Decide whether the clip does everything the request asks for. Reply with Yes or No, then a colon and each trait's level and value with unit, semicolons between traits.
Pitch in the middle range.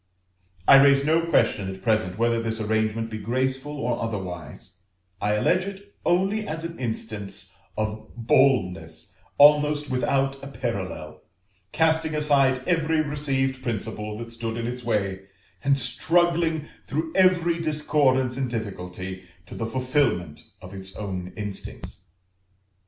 No: low, 125 Hz